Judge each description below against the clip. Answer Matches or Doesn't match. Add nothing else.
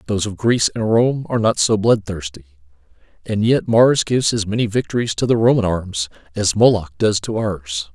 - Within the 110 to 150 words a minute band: Doesn't match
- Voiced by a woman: Doesn't match